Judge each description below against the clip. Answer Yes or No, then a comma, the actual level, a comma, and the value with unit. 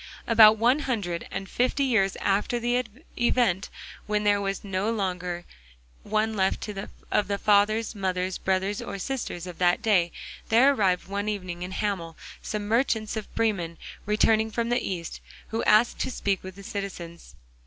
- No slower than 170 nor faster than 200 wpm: No, average, 160 wpm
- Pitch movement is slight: No, average, 3.0 semitones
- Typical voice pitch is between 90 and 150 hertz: No, high, 205 Hz